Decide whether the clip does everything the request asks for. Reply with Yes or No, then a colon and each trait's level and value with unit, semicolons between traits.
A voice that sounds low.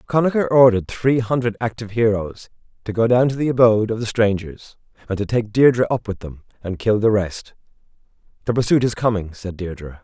Yes: low, 110 Hz